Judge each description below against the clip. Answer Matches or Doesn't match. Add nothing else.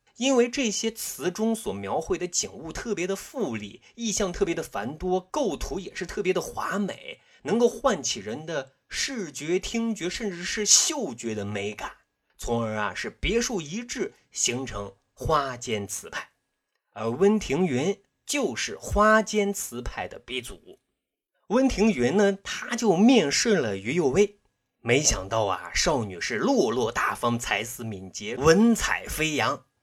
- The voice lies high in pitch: Matches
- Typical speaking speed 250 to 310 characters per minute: Doesn't match